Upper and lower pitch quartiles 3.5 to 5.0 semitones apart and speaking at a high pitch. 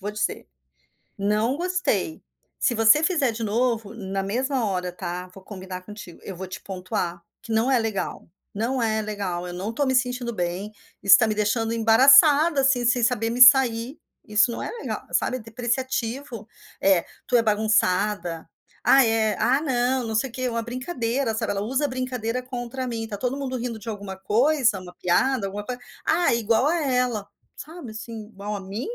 Yes: average, 3.8 semitones; high, 225 Hz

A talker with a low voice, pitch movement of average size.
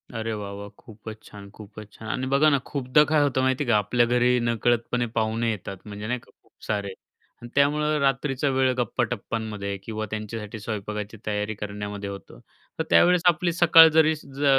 Yes: low, 115 Hz; average, 4.4 semitones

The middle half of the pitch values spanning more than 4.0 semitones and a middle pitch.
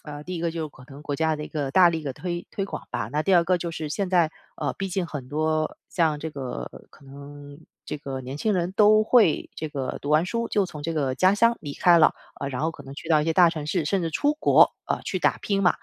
No: average, 3.7 semitones; medium, 160 Hz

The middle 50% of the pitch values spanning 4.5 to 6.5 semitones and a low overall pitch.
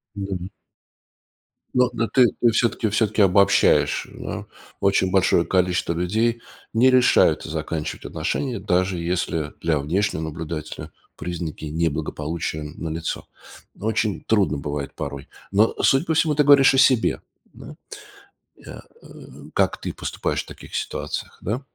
Yes: wide, 5.6 semitones; very low, 95 Hz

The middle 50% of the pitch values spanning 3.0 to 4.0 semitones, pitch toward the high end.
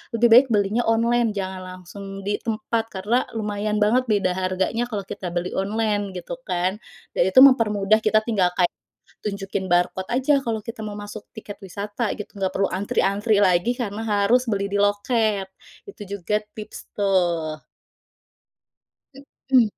No: narrow, 2.6 semitones; high, 205 Hz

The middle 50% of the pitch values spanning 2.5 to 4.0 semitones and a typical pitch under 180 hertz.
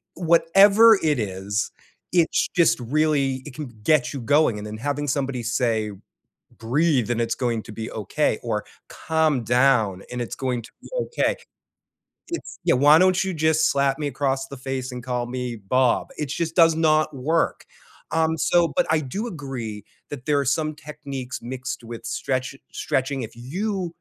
No: average, 4.4 semitones; low, 135 Hz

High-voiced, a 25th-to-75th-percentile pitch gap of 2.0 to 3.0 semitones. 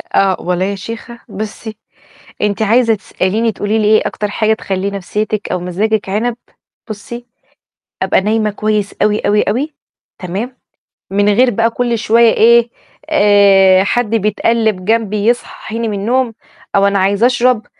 Yes: high, 215 Hz; narrow, 2.5 semitones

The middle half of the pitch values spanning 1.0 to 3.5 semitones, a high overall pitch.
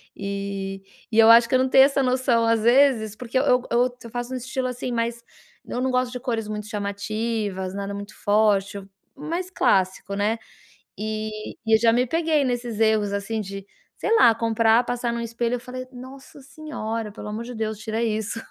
Yes: average, 2.8 semitones; high, 230 Hz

